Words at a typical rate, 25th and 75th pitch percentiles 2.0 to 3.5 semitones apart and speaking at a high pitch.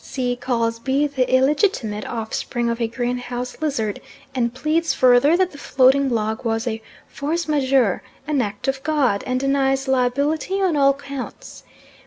Yes: average, 155 wpm; average, 2.9 semitones; very high, 260 Hz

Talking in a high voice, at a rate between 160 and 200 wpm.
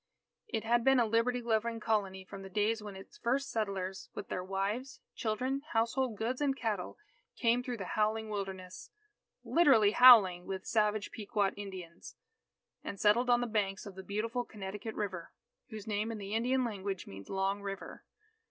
Yes: high, 215 Hz; average, 170 wpm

